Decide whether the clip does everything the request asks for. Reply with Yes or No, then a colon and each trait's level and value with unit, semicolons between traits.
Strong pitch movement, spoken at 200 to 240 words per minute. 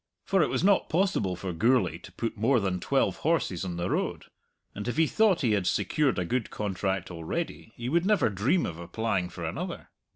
Yes: wide, 8.9 semitones; fast, 205 wpm